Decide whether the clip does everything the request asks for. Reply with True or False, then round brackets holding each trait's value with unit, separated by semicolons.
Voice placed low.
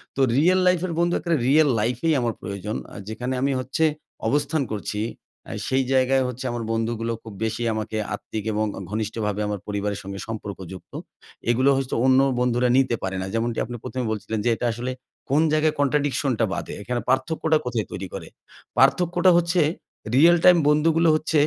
True (125 Hz)